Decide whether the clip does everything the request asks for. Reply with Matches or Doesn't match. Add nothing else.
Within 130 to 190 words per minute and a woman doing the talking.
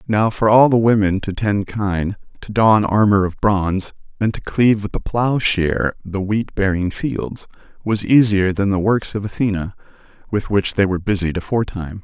Doesn't match